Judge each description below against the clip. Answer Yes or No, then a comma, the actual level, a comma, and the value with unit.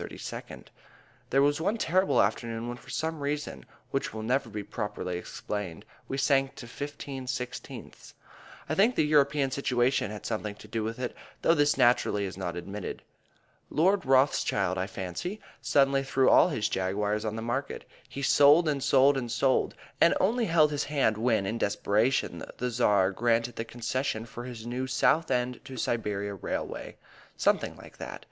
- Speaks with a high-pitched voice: No, low, 125 Hz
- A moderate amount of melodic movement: Yes, average, 4.7 semitones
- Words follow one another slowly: No, average, 165 wpm